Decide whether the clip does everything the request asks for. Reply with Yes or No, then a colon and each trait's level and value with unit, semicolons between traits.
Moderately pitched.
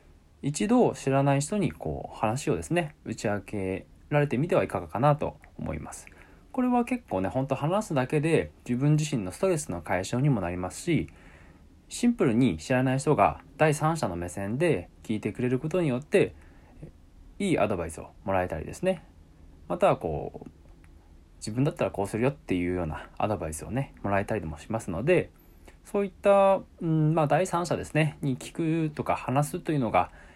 No: low, 125 Hz